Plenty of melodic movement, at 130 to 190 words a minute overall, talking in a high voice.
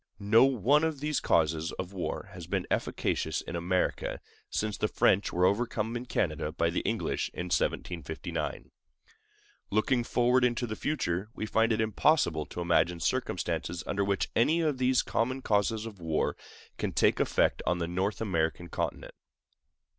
No: wide, 5.8 semitones; average, 160 wpm; low, 100 Hz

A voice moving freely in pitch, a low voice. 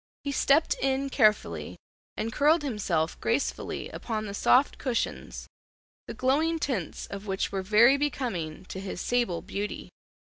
No: wide, 6.0 semitones; high, 230 Hz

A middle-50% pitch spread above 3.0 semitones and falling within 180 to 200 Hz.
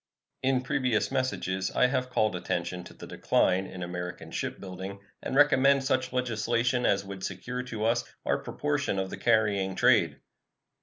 No: average, 5.2 semitones; low, 115 Hz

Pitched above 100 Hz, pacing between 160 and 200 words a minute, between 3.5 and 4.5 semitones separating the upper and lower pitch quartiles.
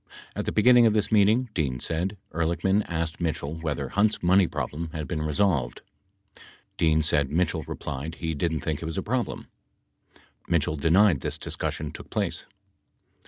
No: very low, 85 Hz; average, 165 wpm; average, 4.0 semitones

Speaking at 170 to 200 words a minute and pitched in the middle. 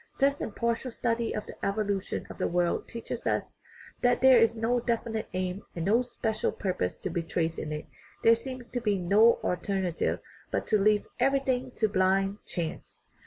No: average, 185 wpm; high, 215 Hz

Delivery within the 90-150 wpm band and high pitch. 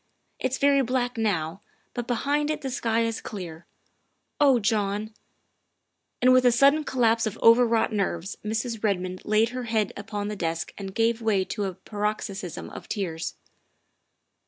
No: average, 160 wpm; high, 220 Hz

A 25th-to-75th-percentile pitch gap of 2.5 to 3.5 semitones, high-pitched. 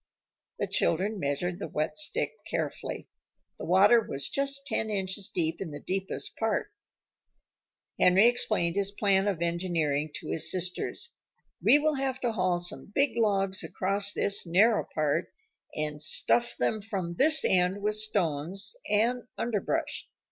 No: average, 4.2 semitones; high, 195 Hz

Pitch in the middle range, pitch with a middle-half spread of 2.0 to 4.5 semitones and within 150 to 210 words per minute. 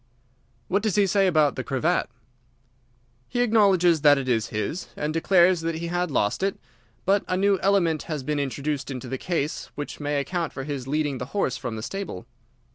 No: medium, 155 Hz; average, 5.1 semitones; average, 195 wpm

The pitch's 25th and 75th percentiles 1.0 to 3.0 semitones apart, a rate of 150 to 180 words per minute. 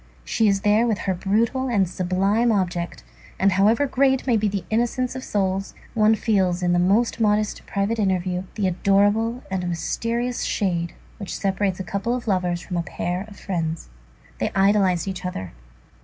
No: average, 3.4 semitones; average, 170 wpm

